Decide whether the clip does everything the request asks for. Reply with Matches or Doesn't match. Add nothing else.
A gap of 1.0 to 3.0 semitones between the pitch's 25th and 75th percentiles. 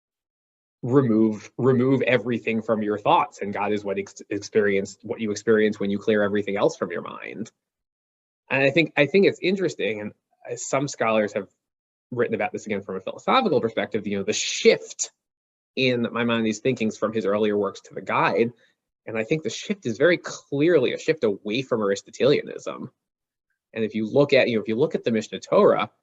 Doesn't match